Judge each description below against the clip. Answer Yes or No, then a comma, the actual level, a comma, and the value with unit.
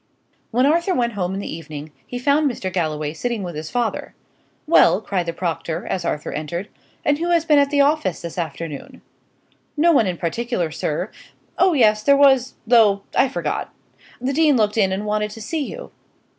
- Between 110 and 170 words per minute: No, average, 190 wpm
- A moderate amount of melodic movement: No, wide, 8.4 semitones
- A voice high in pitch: Yes, high, 215 Hz